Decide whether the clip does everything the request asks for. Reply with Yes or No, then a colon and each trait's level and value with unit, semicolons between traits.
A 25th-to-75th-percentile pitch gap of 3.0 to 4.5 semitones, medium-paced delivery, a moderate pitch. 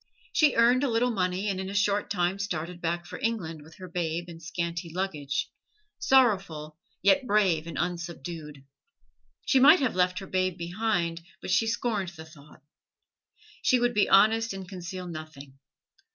Yes: average, 4.0 semitones; average, 165 wpm; medium, 180 Hz